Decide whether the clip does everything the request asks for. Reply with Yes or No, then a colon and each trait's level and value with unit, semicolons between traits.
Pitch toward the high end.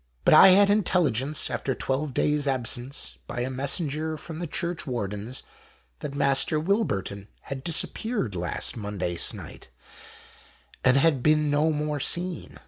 No: medium, 145 Hz